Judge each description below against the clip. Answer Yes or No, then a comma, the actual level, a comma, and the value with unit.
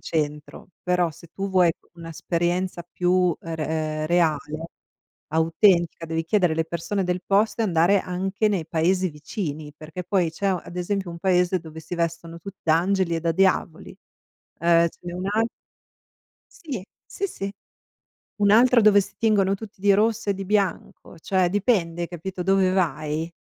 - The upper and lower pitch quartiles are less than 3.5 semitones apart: Yes, average, 2.9 semitones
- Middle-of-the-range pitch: Yes, medium, 180 Hz